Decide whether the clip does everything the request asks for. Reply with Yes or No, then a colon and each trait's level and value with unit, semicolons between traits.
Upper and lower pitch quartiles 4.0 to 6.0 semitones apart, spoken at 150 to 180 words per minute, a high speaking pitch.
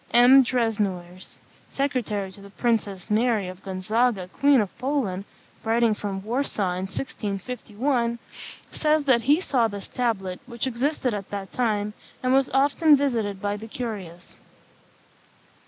No: average, 4.4 semitones; slow, 135 wpm; high, 225 Hz